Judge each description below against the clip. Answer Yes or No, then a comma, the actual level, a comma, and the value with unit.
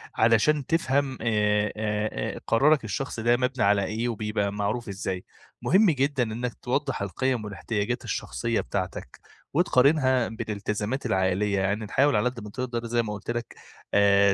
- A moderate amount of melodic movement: Yes, average, 3.8 semitones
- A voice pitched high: No, low, 115 Hz